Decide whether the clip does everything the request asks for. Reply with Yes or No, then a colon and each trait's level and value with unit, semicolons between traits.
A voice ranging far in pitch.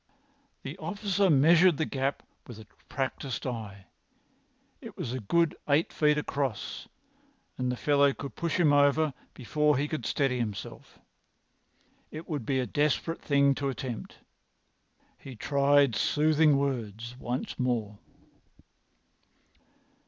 No: average, 3.2 semitones